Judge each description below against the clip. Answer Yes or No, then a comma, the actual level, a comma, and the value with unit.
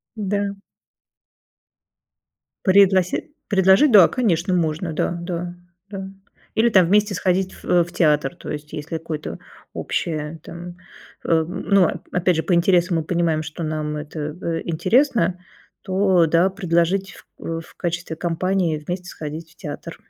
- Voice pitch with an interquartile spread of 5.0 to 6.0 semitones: No, average, 2.9 semitones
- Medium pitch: Yes, medium, 175 Hz